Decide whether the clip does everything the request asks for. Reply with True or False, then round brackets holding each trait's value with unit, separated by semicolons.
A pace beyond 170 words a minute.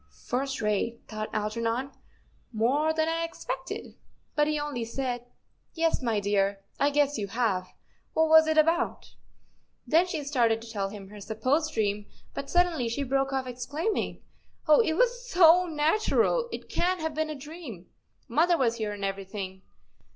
False (165 wpm)